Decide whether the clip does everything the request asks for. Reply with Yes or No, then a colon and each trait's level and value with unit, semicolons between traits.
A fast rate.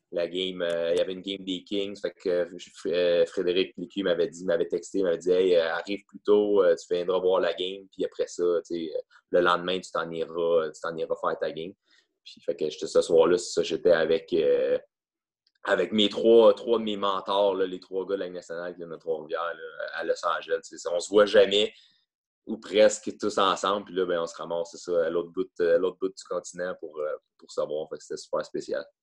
Yes: fast, 230 wpm